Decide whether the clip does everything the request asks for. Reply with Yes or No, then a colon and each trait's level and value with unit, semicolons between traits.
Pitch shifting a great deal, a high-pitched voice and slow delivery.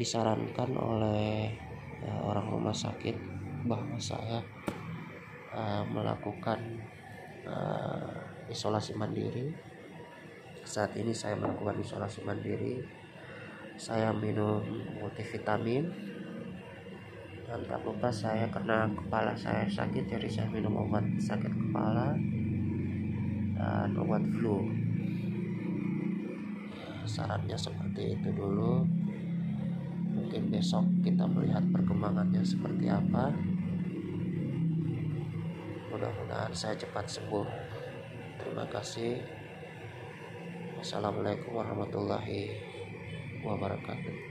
No: wide, 8.2 semitones; low, 125 Hz; slow, 80 wpm